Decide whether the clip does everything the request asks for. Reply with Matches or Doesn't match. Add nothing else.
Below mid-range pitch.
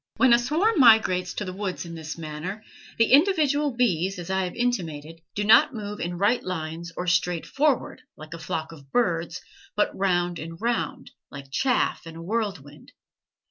Doesn't match